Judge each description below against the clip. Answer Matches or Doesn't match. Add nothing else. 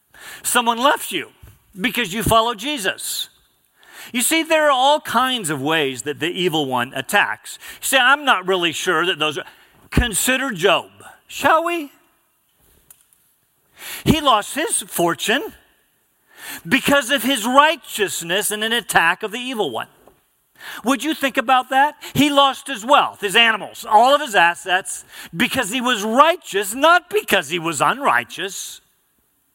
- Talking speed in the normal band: Matches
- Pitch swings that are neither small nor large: Doesn't match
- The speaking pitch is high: Matches